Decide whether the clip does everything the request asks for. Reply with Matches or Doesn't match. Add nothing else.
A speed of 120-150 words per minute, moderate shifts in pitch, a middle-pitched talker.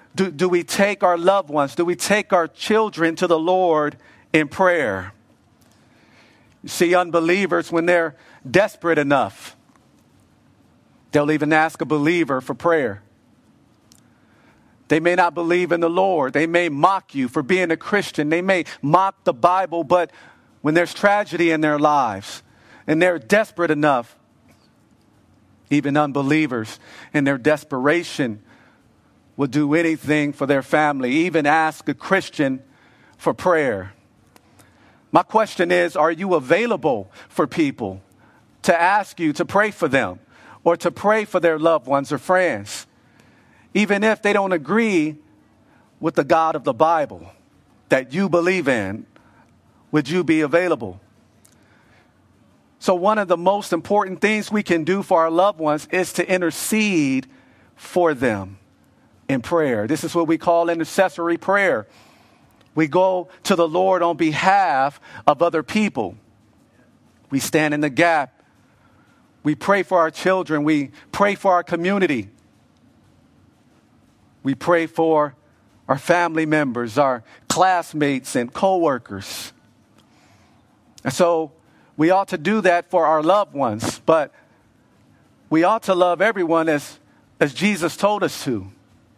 Matches